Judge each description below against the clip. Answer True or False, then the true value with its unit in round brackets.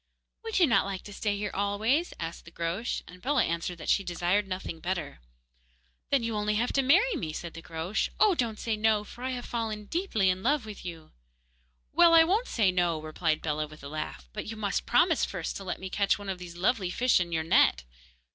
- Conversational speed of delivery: False (225 wpm)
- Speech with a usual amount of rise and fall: False (5.8 semitones)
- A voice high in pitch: True (200 Hz)